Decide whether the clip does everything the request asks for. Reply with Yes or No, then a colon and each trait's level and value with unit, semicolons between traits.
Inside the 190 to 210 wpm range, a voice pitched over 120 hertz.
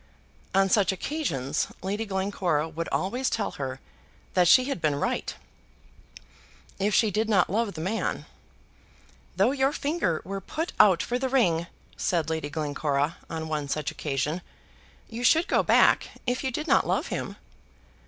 No: average, 155 wpm; high, 190 Hz